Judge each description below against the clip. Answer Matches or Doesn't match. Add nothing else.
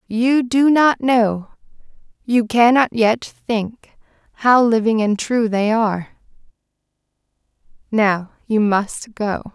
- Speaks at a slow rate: Matches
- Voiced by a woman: Matches